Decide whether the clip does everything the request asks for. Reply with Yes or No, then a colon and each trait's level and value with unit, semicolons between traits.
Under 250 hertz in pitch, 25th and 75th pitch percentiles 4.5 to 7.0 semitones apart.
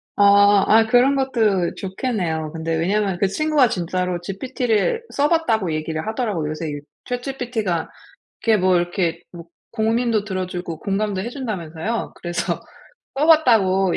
Yes: high, 200 Hz; wide, 5.5 semitones